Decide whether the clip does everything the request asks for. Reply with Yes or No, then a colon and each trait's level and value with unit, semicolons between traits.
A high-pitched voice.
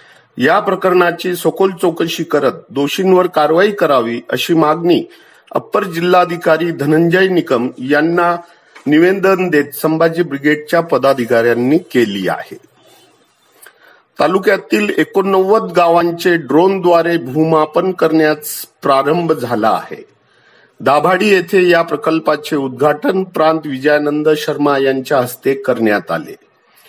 No: medium, 160 Hz